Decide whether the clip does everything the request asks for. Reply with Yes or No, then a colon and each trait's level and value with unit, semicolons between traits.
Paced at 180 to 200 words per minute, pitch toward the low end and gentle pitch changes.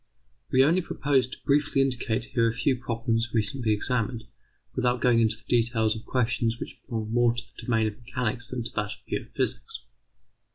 Yes: average, 190 wpm; low, 120 Hz; narrow, 2.1 semitones